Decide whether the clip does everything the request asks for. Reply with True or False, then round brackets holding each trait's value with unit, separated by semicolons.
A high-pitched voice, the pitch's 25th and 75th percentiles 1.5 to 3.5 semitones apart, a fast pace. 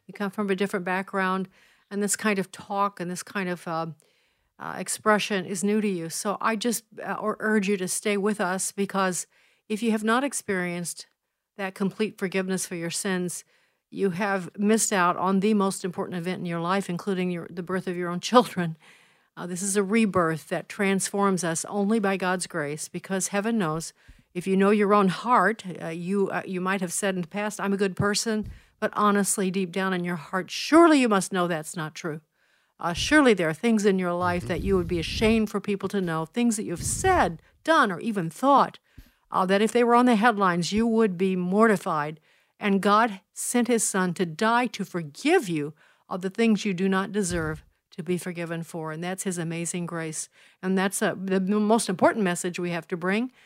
True (195 Hz; 2.9 semitones; 210 wpm)